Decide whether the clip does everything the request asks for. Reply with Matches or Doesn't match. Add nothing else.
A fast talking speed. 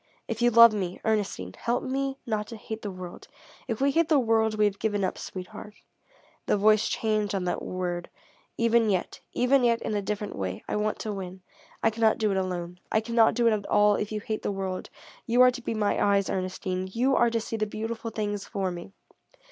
Matches